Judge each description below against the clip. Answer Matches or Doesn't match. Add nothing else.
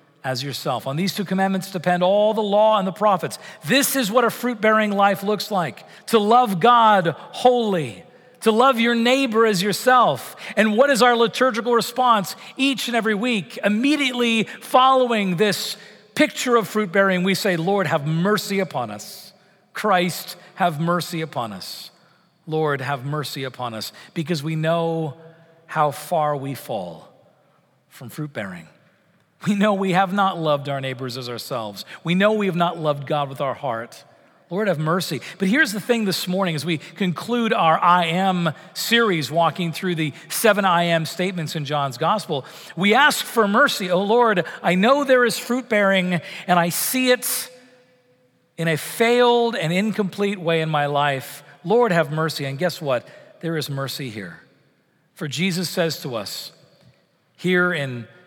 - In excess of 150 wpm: Matches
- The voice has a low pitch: Doesn't match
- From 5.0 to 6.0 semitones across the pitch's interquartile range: Matches